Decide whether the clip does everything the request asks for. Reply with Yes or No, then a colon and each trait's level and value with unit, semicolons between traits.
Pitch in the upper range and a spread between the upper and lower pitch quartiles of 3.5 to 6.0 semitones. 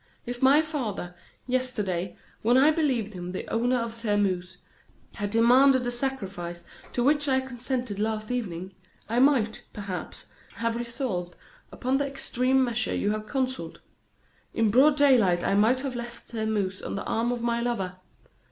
Yes: high, 235 Hz; average, 4.1 semitones